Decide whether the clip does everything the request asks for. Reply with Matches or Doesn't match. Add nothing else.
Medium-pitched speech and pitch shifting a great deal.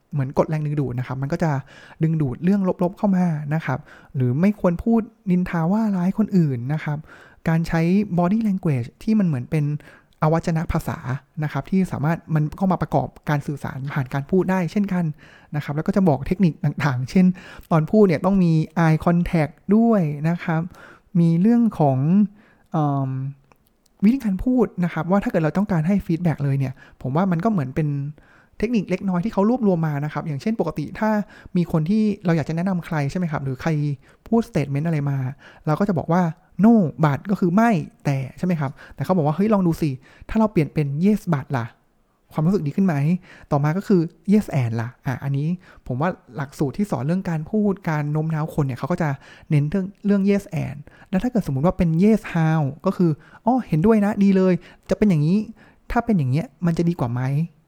Doesn't match